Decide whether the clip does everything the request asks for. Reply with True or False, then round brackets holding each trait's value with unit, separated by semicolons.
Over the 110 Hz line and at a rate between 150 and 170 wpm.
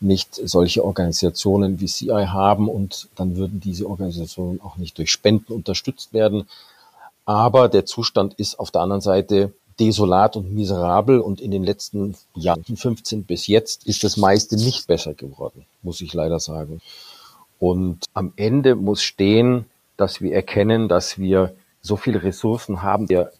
False (100 Hz; 155 wpm)